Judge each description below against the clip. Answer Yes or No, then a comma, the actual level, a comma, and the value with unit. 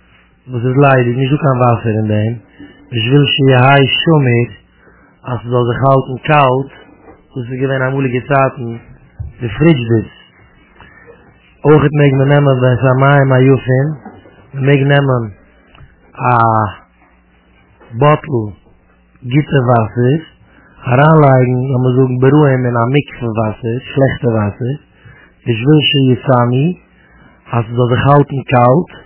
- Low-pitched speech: Yes, low, 130 Hz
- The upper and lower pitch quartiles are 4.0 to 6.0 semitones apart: No, average, 2.7 semitones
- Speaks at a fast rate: No, average, 145 wpm